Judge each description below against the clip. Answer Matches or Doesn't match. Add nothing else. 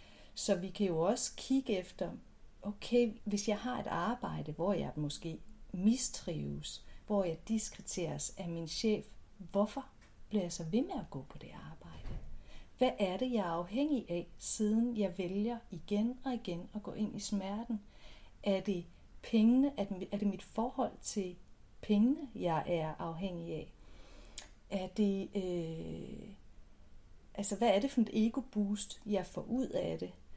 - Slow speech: Doesn't match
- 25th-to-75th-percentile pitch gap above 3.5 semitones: Matches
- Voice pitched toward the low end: Doesn't match